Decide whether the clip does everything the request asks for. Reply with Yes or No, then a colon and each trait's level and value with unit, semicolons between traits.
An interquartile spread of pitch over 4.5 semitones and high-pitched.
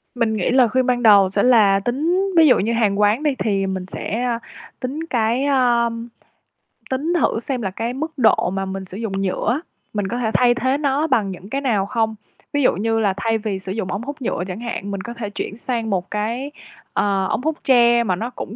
No: average, 4.2 semitones; high, 230 Hz